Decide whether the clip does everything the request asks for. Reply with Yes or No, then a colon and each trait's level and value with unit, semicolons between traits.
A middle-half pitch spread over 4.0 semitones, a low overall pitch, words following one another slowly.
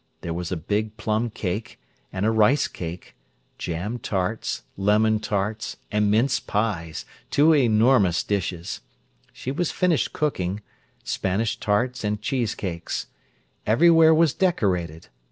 Yes: average, 4.6 semitones; low, 105 Hz; slow, 120 wpm